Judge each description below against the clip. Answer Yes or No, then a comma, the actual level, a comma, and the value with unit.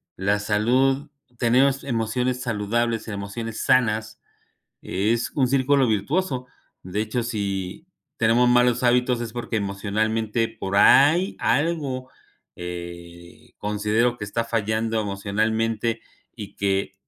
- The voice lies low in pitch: Yes, low, 115 Hz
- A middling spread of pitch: Yes, average, 3.2 semitones